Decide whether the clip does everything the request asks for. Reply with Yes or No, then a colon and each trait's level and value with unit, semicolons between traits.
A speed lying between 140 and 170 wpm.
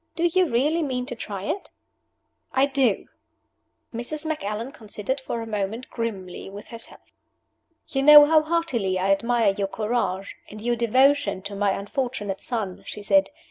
Yes: average, 155 wpm